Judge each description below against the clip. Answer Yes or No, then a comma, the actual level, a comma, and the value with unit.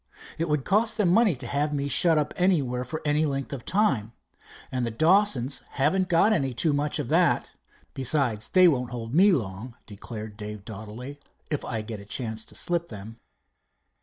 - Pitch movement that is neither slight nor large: No, wide, 6.3 semitones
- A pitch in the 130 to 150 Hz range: Yes, medium, 140 Hz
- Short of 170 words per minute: No, average, 185 wpm